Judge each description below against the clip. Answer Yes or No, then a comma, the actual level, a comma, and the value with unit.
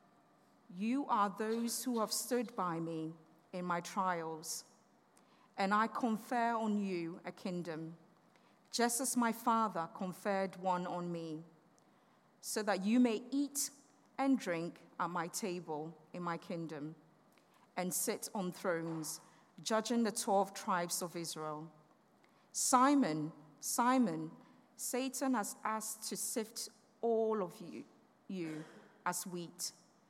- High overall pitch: Yes, high, 195 Hz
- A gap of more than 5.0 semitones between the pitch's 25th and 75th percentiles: Yes, wide, 5.4 semitones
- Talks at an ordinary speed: No, slow, 125 wpm